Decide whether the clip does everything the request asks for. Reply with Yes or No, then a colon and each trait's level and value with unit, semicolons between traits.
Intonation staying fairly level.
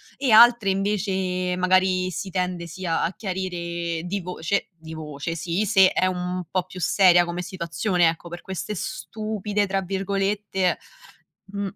Yes: narrow, 2.2 semitones